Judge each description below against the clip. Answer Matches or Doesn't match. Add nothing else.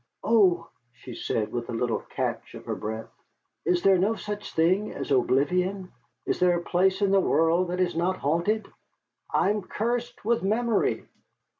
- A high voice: Doesn't match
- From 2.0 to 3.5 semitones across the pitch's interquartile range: Doesn't match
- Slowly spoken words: Doesn't match